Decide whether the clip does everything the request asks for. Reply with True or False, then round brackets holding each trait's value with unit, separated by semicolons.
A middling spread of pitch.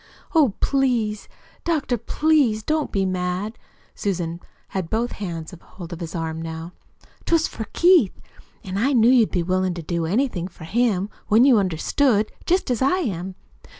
False (6.1 semitones)